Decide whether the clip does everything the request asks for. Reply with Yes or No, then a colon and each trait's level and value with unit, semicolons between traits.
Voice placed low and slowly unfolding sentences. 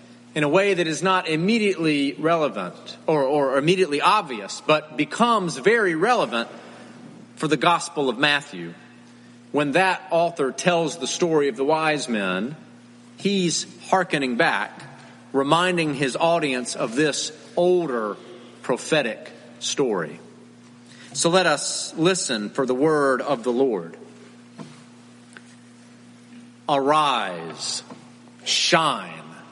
No: medium, 145 Hz; slow, 110 wpm